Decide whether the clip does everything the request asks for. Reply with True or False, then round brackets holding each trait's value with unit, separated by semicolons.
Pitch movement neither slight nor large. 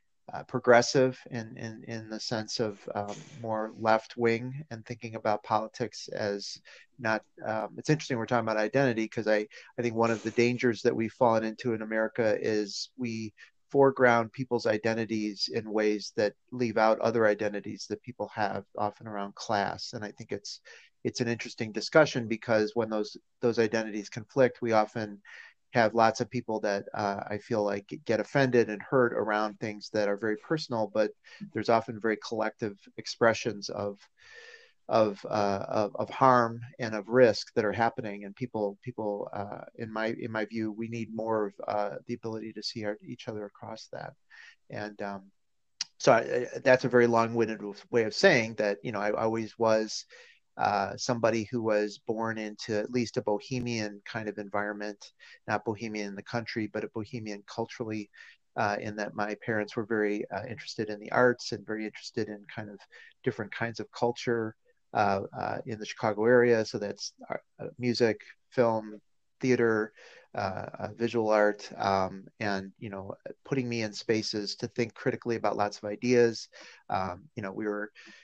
False (2.1 semitones)